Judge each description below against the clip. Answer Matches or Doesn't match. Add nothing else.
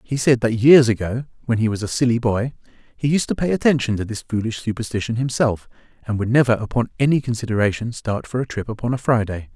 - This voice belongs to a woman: Doesn't match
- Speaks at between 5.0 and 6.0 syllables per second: Doesn't match